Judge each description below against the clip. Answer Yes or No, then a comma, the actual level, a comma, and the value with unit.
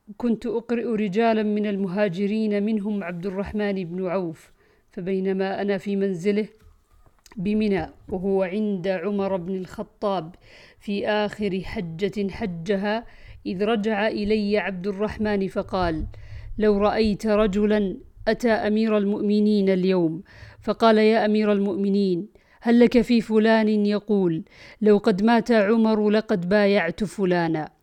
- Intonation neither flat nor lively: No, narrow, 1.9 semitones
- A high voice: Yes, high, 205 Hz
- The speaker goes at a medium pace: Yes, average, 115 wpm